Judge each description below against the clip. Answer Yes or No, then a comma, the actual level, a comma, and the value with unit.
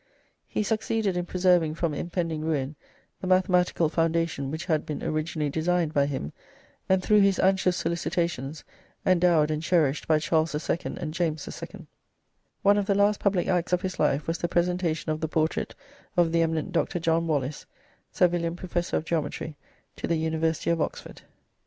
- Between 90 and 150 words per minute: No, average, 170 wpm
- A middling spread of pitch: No, narrow, 2.3 semitones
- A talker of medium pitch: Yes, medium, 165 Hz